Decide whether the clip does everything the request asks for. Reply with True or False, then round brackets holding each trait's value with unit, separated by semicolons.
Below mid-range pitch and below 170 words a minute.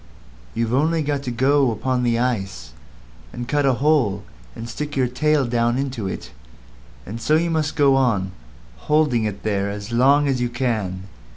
False (125 Hz; 175 wpm)